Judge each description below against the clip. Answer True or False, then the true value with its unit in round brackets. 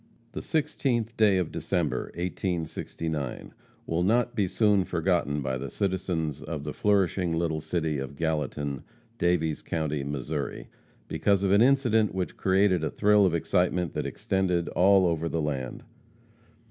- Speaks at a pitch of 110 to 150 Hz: False (85 Hz)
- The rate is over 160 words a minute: False (145 wpm)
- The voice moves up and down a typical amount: True (4.1 semitones)